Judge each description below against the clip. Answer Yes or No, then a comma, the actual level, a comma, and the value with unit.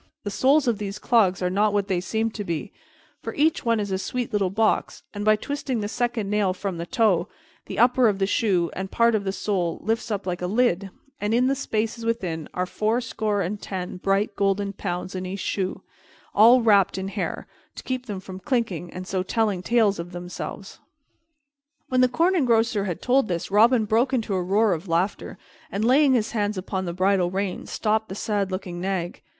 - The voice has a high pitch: Yes, high, 205 Hz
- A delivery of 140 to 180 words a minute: No, fast, 205 wpm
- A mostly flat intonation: No, average, 3.4 semitones